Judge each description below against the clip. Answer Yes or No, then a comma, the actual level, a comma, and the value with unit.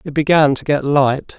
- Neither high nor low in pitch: Yes, medium, 145 Hz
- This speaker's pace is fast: Yes, fast, 215 wpm